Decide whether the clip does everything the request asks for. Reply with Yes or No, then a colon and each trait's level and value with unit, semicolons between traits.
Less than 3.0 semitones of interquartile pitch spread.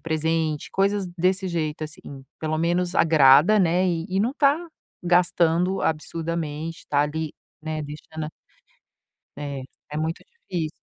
Yes: narrow, 2.6 semitones